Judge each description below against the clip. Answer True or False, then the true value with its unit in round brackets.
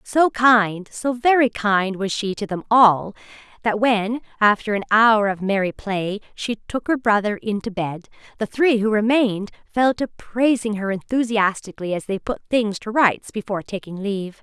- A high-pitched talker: True (215 Hz)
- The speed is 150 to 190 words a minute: True (180 wpm)